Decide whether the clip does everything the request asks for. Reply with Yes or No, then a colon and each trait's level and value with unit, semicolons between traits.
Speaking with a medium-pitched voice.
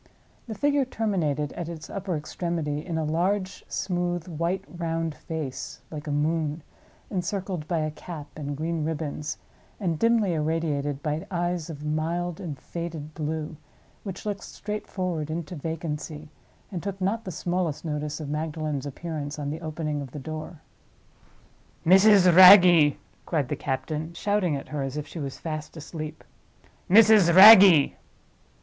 Yes: medium, 160 Hz